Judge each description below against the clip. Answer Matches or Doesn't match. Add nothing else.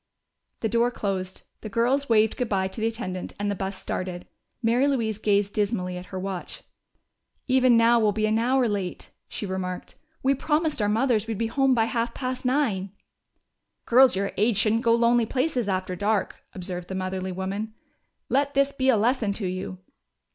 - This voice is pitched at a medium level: Doesn't match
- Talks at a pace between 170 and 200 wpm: Matches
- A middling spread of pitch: Matches